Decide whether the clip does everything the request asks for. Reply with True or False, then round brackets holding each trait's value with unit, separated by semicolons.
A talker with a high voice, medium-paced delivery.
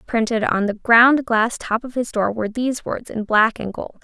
False (230 Hz; 240 wpm)